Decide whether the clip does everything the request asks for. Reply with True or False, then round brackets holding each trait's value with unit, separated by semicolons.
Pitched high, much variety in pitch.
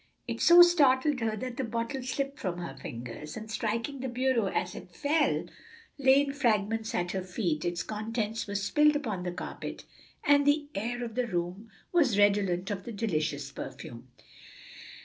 True (225 Hz; 6.2 semitones)